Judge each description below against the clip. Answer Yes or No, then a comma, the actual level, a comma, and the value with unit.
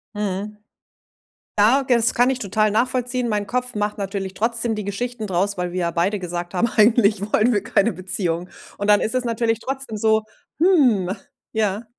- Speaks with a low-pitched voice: No, high, 215 Hz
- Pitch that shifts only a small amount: No, average, 3.3 semitones